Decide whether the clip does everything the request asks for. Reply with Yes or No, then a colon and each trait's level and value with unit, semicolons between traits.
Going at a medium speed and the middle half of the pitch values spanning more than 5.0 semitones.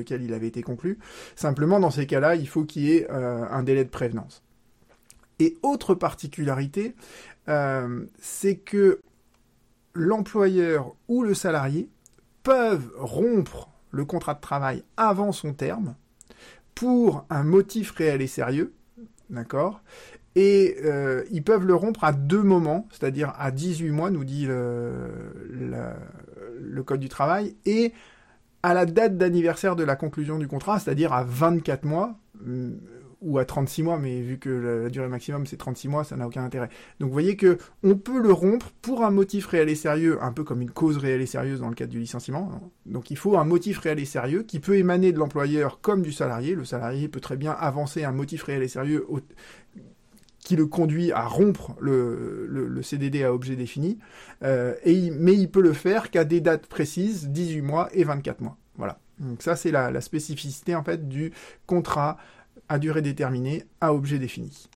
Yes: average, 190 wpm; wide, 5.5 semitones